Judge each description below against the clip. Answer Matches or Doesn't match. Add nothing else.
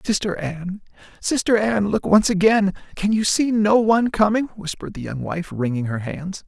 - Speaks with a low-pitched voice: Doesn't match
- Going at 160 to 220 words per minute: Matches